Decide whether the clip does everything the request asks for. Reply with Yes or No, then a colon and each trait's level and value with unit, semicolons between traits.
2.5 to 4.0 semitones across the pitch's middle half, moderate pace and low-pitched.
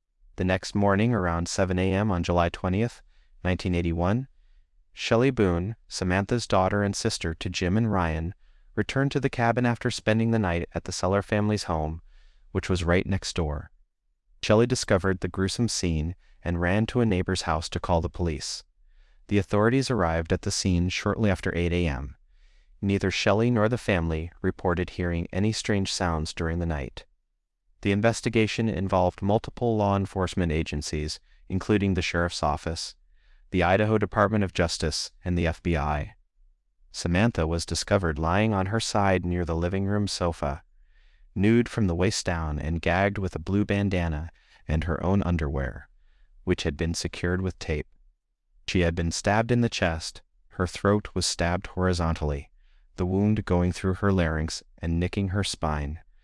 Yes: average, 3.4 semitones; average, 165 wpm; very low, 90 Hz